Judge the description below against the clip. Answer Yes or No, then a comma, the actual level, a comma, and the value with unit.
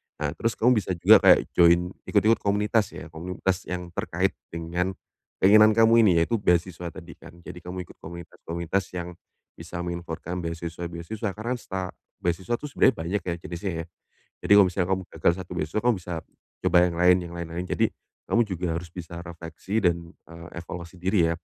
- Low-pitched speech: Yes, very low, 90 Hz